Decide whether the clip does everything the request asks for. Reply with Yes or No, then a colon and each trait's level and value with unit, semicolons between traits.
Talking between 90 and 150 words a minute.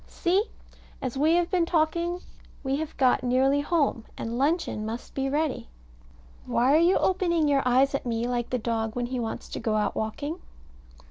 No: average, 185 wpm